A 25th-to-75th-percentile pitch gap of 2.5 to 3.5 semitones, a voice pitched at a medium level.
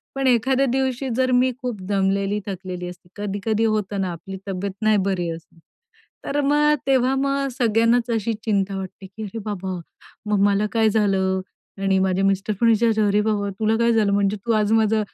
No: average, 3.2 semitones; high, 210 Hz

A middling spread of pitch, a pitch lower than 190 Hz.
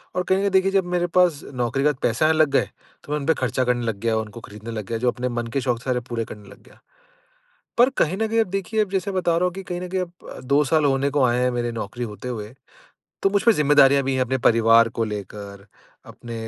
No: wide, 7.2 semitones; low, 135 Hz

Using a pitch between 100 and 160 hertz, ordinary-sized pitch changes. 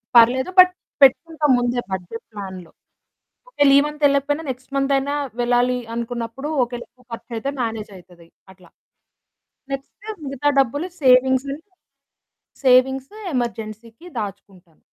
No: very high, 250 Hz; average, 3.6 semitones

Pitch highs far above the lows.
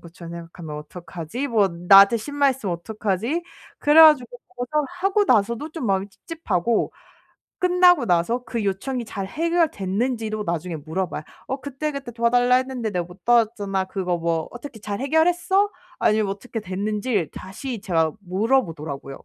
Yes: wide, 6.4 semitones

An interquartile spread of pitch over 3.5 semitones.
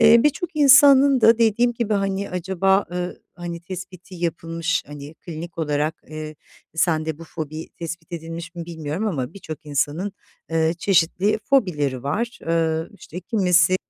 Yes: average, 3.9 semitones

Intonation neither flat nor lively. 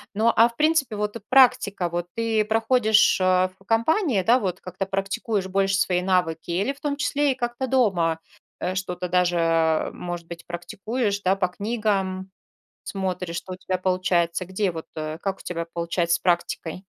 Yes: average, 4.2 semitones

